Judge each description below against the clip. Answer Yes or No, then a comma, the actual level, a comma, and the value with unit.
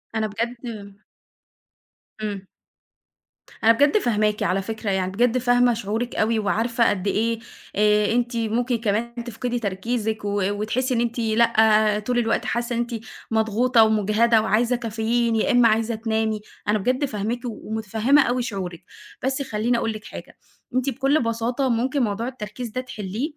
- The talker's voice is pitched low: No, high, 225 Hz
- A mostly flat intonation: Yes, narrow, 2.2 semitones